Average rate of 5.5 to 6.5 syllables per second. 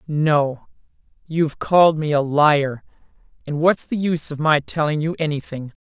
No: 4.8 syllables/s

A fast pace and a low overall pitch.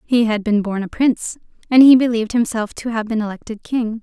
No: fast, 225 wpm; high, 225 Hz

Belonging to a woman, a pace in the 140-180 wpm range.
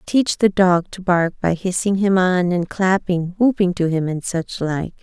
No: female; fast, 205 wpm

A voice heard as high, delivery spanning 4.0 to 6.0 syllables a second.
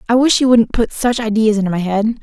No: high, 225 Hz; 6.2 syllables/s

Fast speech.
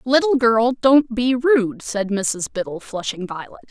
No: average, 160 wpm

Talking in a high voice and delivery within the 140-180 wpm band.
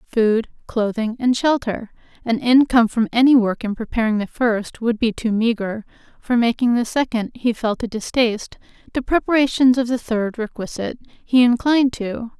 Yes: high, 235 Hz; average, 165 wpm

